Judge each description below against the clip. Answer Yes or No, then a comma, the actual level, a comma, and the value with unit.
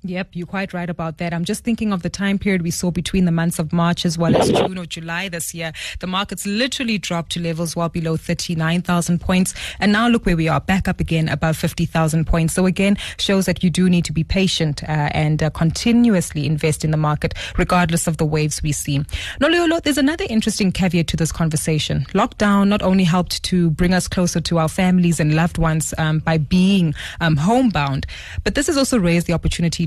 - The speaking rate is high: Yes, fast, 215 wpm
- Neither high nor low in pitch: Yes, medium, 175 Hz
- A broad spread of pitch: No, average, 2.7 semitones